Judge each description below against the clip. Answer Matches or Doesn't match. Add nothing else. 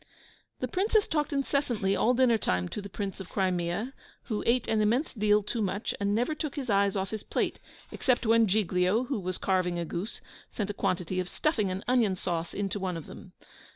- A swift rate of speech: Matches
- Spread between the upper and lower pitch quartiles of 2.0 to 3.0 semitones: Doesn't match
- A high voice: Matches